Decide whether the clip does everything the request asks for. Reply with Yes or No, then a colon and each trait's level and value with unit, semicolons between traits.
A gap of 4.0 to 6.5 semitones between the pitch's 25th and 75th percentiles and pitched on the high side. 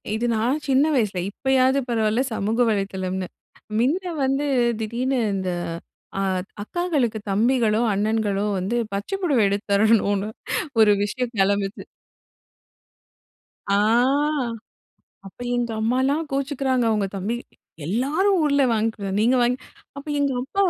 Yes: average, 4.5 semitones; high, 230 Hz